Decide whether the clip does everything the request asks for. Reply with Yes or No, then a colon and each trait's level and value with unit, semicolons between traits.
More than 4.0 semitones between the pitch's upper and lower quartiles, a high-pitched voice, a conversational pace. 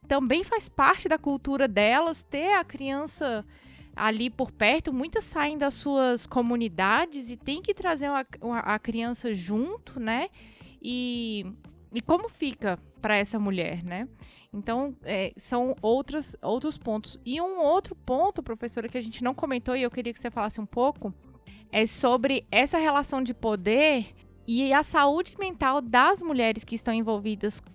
Yes: average, 4.4 semitones; very high, 250 Hz; average, 160 wpm